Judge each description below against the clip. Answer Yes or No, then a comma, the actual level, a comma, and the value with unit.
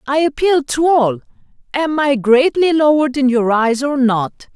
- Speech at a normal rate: Yes, average, 170 wpm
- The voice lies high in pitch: Yes, very high, 270 Hz